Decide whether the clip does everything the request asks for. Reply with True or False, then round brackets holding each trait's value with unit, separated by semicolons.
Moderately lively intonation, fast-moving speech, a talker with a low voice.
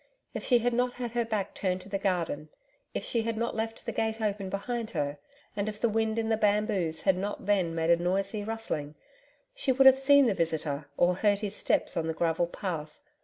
False (4.5 semitones; 220 wpm; 205 Hz)